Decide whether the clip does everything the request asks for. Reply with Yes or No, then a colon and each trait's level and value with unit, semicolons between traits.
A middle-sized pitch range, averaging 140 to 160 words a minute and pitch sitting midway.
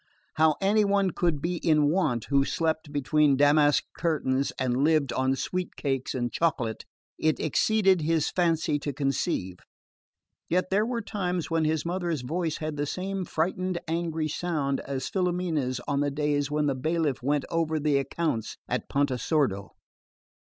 Yes: average, 3.6 semitones; average, 155 wpm; medium, 155 Hz